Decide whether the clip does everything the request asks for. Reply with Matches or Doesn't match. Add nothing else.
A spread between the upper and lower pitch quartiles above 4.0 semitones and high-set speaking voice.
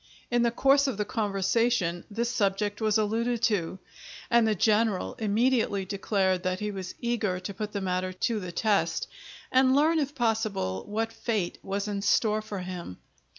Doesn't match